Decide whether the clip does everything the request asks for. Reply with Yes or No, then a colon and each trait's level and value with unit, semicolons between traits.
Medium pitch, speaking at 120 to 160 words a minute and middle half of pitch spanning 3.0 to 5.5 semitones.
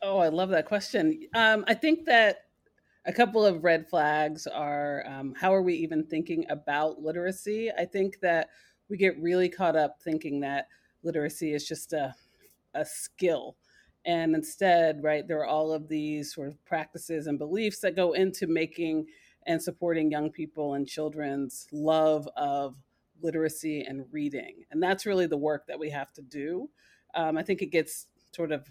No: medium, 160 Hz; average, 175 wpm; average, 3.6 semitones